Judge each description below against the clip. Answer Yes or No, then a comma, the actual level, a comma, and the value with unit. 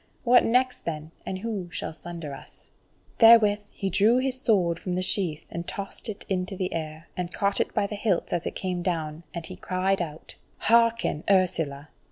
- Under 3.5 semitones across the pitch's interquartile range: No, average, 3.8 semitones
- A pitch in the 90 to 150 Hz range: No, medium, 185 Hz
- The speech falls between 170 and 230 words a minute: Yes, average, 190 wpm